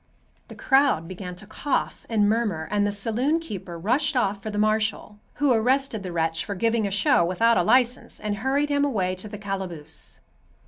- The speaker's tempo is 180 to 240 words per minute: Yes, average, 190 wpm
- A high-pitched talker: Yes, high, 210 Hz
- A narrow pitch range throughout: No, average, 4.7 semitones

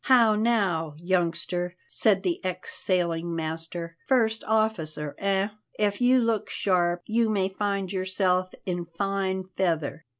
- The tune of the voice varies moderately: Yes, average, 3.3 semitones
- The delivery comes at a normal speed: No, slow, 130 wpm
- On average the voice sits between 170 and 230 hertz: Yes, medium, 185 Hz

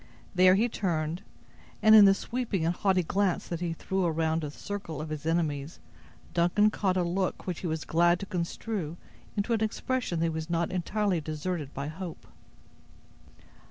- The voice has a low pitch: No, medium, 175 Hz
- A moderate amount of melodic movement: Yes, average, 3.4 semitones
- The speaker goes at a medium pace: Yes, average, 175 wpm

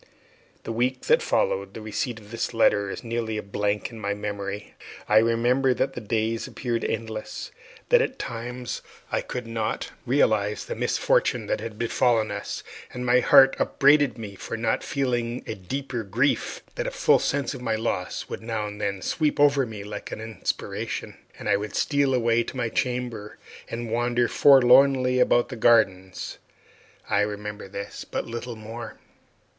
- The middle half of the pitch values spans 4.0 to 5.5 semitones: No, average, 2.9 semitones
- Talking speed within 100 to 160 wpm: No, average, 170 wpm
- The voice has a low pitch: Yes, low, 115 Hz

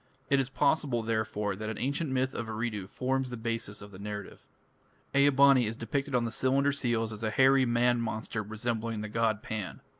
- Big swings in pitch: No, average, 3.3 semitones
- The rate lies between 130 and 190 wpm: No, average, 200 wpm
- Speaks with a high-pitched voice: No, low, 115 Hz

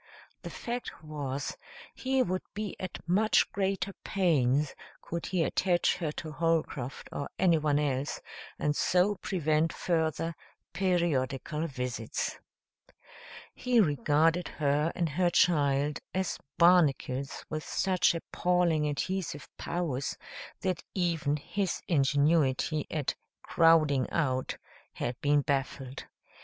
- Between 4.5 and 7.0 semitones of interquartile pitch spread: No, average, 3.9 semitones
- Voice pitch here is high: No, medium, 160 Hz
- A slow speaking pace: Yes, slow, 110 wpm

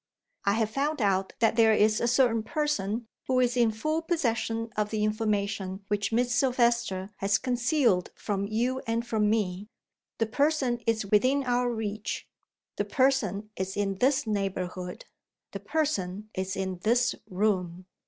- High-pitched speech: Yes, high, 220 Hz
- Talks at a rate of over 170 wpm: No, average, 155 wpm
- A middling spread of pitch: Yes, average, 3.6 semitones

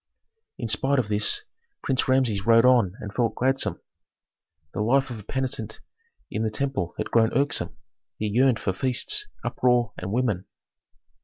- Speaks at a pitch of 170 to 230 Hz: No, low, 120 Hz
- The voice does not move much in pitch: No, average, 3.5 semitones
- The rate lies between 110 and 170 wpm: Yes, average, 155 wpm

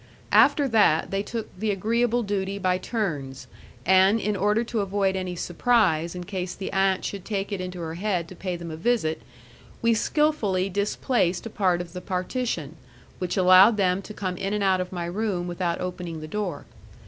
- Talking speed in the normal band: Yes, average, 190 wpm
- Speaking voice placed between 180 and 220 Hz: Yes, high, 190 Hz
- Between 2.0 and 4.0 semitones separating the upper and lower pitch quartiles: Yes, average, 2.8 semitones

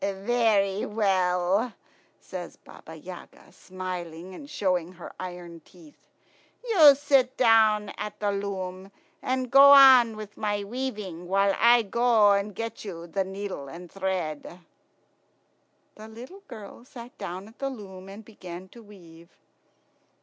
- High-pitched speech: Yes, high, 200 Hz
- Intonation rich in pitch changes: No, average, 3.9 semitones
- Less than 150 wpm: Yes, slow, 135 wpm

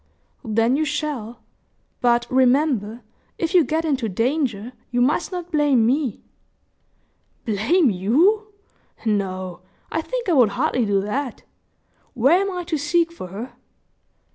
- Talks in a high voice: Yes, very high, 260 Hz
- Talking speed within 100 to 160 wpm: Yes, slow, 135 wpm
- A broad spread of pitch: Yes, wide, 6.2 semitones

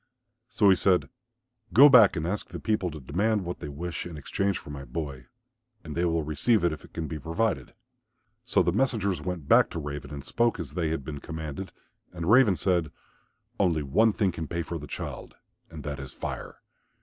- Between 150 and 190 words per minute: No, fast, 205 wpm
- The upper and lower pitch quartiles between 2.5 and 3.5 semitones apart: No, average, 4.6 semitones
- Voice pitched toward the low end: Yes, very low, 85 Hz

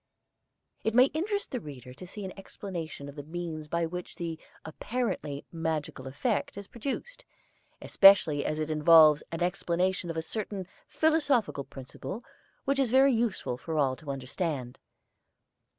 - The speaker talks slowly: No, average, 150 wpm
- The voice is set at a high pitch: No, medium, 170 Hz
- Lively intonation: Yes, wide, 6.7 semitones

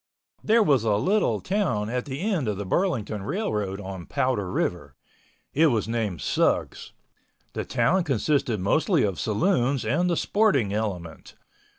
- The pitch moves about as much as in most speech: No, wide, 9.0 semitones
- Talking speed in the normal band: Yes, average, 155 wpm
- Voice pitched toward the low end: Yes, low, 120 Hz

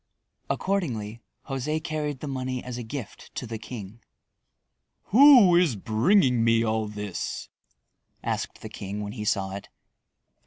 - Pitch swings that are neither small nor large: No, wide, 5.9 semitones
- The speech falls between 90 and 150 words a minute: Yes, average, 140 wpm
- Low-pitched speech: Yes, low, 120 Hz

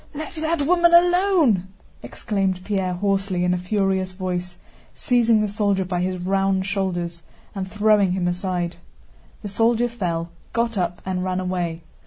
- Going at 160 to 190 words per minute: No, average, 150 wpm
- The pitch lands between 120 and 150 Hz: No, high, 190 Hz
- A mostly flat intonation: No, average, 3.2 semitones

